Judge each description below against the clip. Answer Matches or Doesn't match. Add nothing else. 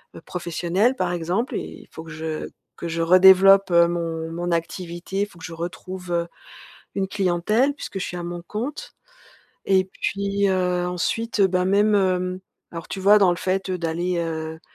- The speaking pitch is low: Doesn't match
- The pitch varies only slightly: Matches